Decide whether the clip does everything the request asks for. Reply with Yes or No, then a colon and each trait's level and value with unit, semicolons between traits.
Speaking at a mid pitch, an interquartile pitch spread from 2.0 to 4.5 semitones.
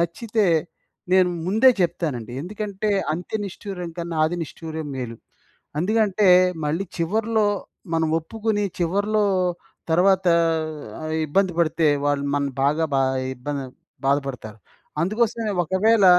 No: medium, 175 Hz; average, 5.0 semitones